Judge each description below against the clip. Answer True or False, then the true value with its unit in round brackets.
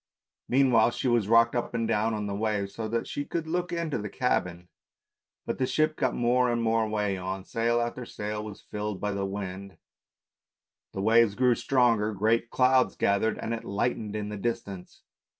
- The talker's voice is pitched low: True (110 Hz)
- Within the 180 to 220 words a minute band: True (185 wpm)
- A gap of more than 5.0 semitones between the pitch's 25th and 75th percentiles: False (2.8 semitones)